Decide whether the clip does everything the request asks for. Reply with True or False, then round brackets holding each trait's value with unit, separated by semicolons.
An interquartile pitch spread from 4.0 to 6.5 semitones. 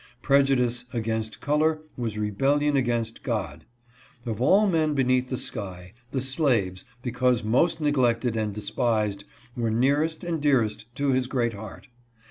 True (4.3 semitones)